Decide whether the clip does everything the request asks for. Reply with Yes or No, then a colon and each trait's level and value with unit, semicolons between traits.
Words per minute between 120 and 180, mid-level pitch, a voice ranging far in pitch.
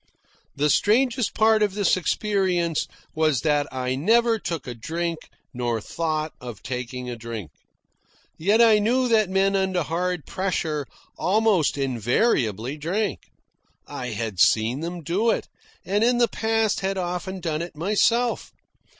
Yes: average, 140 wpm; medium, 175 Hz; wide, 7.5 semitones